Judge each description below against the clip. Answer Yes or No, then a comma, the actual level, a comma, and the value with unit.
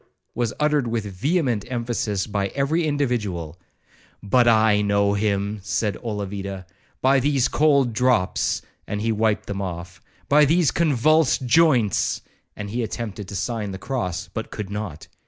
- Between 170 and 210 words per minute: No, average, 140 wpm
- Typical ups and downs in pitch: Yes, average, 4.6 semitones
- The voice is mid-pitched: No, low, 110 Hz